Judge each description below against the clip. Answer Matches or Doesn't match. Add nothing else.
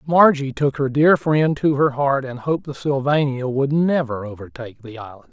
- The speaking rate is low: Doesn't match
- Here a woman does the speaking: Doesn't match